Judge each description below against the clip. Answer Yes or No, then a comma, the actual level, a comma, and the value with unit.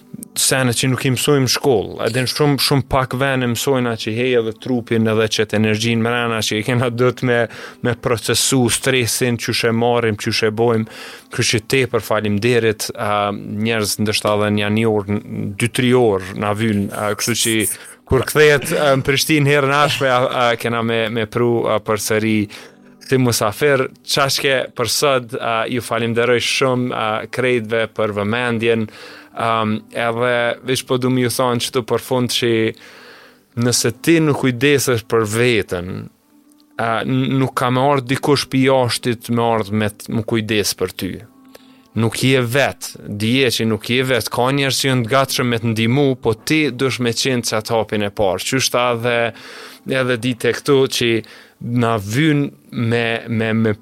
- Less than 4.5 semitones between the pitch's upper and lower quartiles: Yes, average, 2.8 semitones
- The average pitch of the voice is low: Yes, low, 120 Hz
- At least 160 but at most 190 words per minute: Yes, average, 170 wpm